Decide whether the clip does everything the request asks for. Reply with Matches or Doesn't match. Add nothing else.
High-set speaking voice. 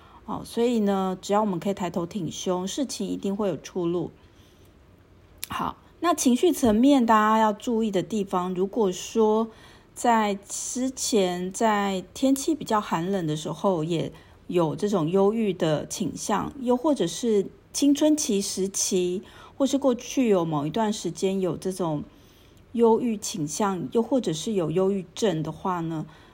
Matches